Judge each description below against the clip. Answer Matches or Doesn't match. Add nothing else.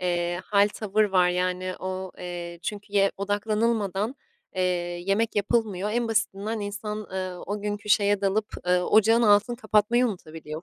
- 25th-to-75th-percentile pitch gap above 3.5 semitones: Doesn't match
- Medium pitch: Doesn't match